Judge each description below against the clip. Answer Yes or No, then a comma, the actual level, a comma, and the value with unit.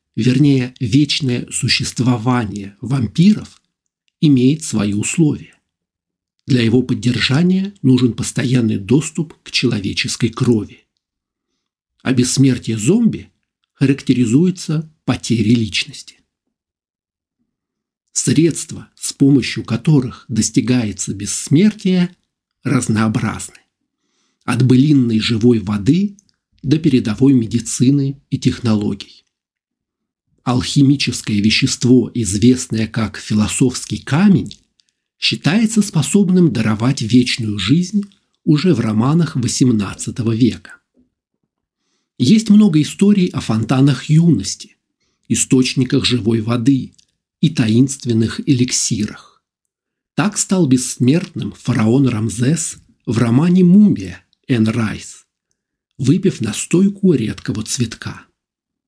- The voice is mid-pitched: No, low, 125 Hz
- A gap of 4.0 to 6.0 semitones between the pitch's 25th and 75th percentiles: Yes, average, 4.3 semitones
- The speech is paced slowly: Yes, slow, 80 wpm